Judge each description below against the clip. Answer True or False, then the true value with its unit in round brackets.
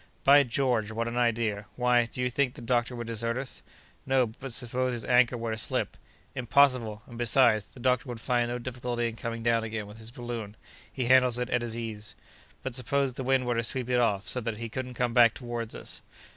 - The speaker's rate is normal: False (225 wpm)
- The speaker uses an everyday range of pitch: False (1.7 semitones)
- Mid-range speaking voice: False (120 Hz)